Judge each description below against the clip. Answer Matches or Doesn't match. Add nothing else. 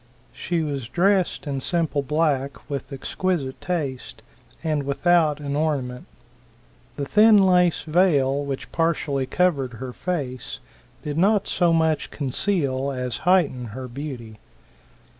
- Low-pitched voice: Doesn't match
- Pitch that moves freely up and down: Doesn't match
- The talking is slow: Matches